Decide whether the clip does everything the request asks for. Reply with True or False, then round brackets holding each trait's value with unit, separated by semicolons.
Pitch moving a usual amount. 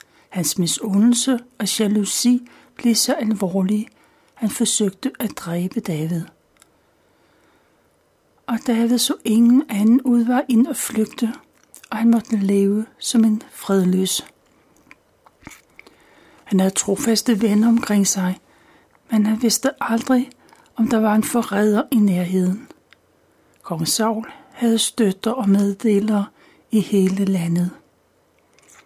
True (3.1 semitones)